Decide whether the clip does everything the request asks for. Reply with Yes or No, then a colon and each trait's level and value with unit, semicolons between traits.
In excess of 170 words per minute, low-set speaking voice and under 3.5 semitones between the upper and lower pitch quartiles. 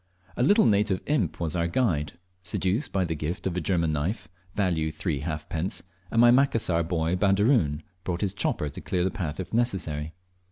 No: average, 185 wpm; very low, 90 Hz; average, 4.2 semitones